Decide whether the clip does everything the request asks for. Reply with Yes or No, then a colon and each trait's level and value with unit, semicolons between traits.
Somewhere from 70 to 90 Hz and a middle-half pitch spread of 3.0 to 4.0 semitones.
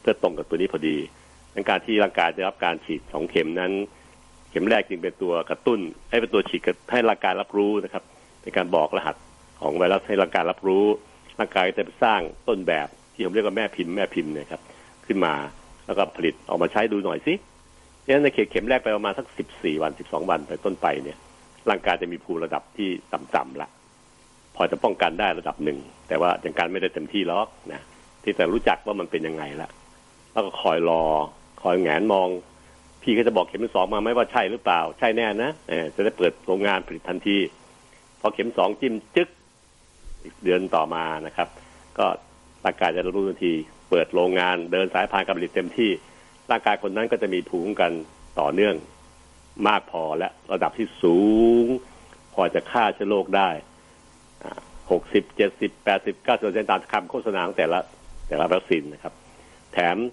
Yes: very low, 85 Hz; average, 3.7 semitones